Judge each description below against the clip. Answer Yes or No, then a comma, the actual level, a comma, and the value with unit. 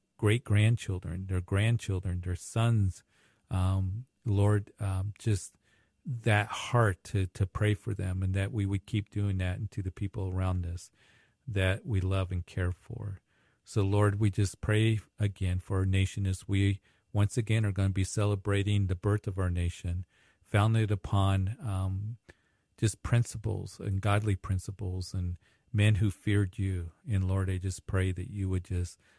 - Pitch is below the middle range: Yes, low, 100 Hz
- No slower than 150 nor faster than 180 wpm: Yes, average, 165 wpm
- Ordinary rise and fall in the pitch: No, narrow, 2.1 semitones